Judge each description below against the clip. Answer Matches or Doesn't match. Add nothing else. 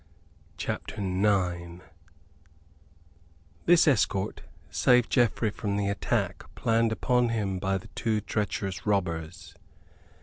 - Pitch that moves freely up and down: Doesn't match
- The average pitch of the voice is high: Doesn't match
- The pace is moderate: Doesn't match